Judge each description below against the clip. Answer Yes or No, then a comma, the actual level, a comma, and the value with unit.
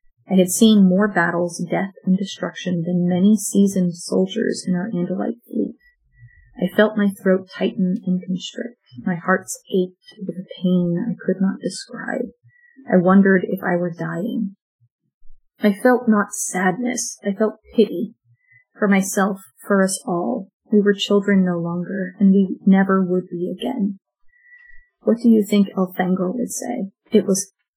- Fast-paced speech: No, average, 155 wpm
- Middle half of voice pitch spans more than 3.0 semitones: No, average, 2.7 semitones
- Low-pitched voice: No, high, 195 Hz